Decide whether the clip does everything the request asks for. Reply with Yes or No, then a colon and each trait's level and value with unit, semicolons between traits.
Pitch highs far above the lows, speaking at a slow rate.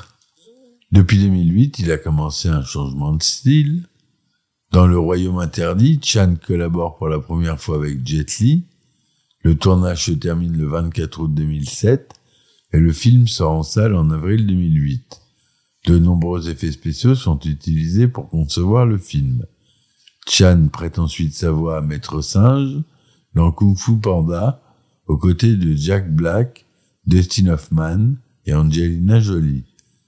Yes: wide, 6.2 semitones; slow, 140 wpm